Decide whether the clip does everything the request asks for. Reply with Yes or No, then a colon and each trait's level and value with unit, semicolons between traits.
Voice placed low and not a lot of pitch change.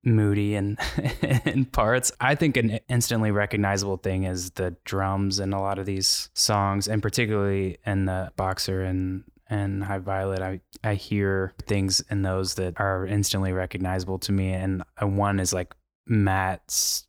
Yes: low, 100 Hz; narrow, 2.0 semitones